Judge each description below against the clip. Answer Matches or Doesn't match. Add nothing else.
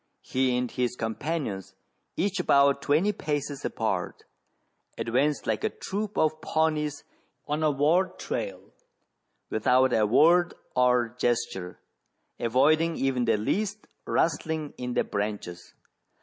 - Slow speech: Matches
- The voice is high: Doesn't match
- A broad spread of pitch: Doesn't match